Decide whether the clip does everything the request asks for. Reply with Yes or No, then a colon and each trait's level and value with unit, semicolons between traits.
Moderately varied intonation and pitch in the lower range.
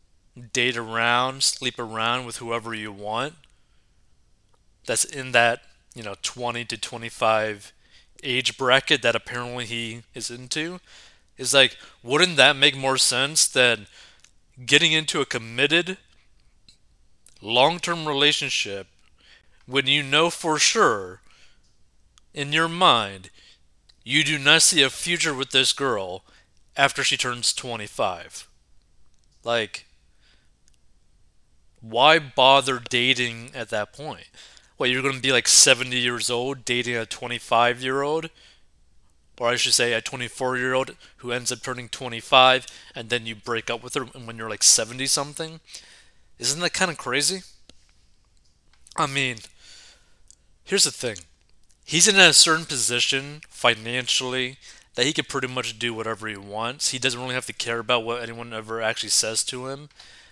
Yes: average, 3.0 semitones; low, 125 Hz